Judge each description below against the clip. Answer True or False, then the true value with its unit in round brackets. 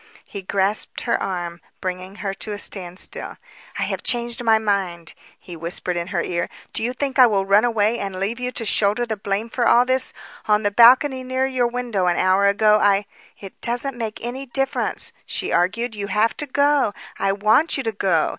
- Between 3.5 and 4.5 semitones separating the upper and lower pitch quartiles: True (3.8 semitones)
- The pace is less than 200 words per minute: False (205 wpm)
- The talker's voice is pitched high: True (210 Hz)